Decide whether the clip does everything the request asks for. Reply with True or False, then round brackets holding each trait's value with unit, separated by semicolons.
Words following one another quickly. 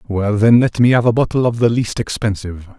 True (235 wpm)